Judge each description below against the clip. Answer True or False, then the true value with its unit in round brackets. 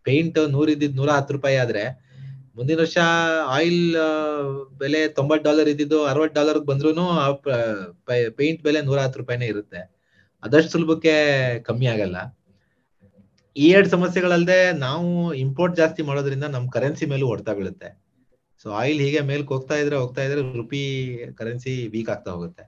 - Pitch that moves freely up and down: False (3.6 semitones)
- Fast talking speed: True (140 wpm)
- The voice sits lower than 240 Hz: True (140 Hz)